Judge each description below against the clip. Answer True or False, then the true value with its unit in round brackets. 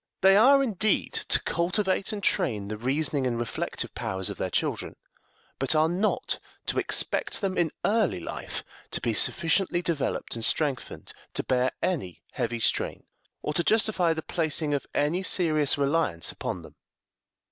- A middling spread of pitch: False (6.3 semitones)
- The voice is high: False (160 Hz)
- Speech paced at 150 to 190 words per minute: True (160 wpm)